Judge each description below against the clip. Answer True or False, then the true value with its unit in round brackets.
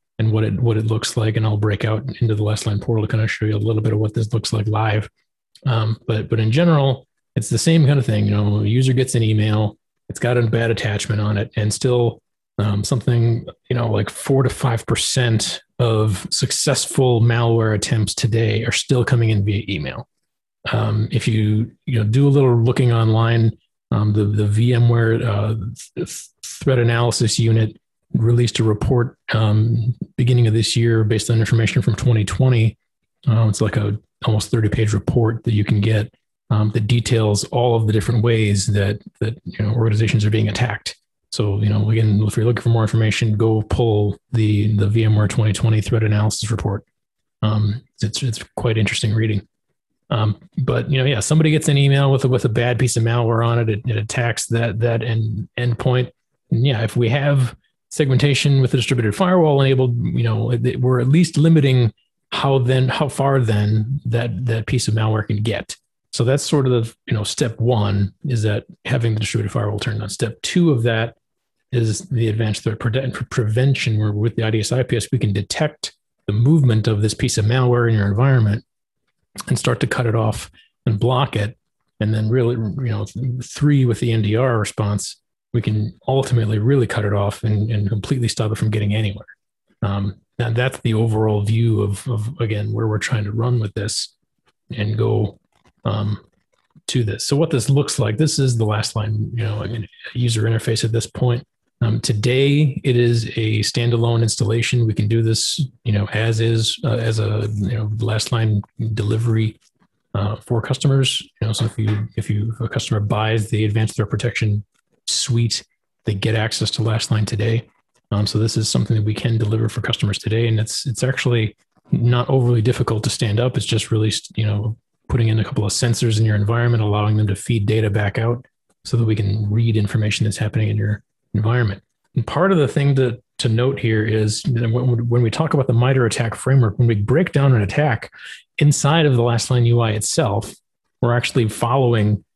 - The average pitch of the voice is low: True (115 Hz)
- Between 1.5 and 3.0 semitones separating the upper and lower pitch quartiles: True (2.4 semitones)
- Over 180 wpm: True (200 wpm)